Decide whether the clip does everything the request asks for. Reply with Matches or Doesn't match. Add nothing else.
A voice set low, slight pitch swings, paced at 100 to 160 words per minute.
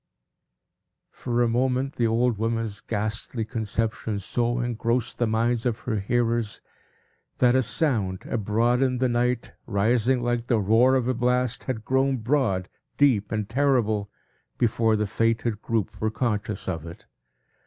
Matches